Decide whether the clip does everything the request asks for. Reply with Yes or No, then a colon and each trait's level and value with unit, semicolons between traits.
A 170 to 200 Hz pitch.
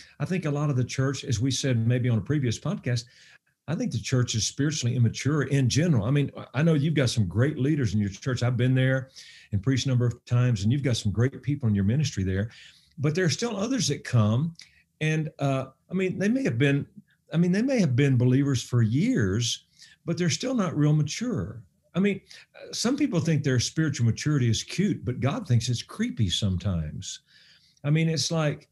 No: low, 135 Hz